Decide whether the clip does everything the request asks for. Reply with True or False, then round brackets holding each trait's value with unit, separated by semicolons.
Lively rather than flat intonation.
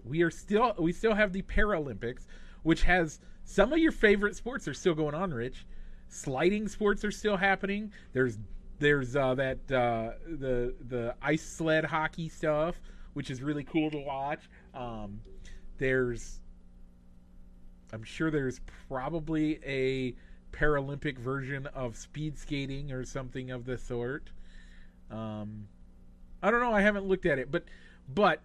True (6.2 semitones)